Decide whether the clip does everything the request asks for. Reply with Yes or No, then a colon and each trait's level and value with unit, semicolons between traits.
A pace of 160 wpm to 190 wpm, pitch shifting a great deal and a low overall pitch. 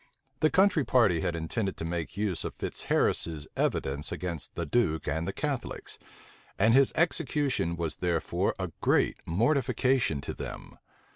No: average, 145 wpm; wide, 8.0 semitones; very low, 95 Hz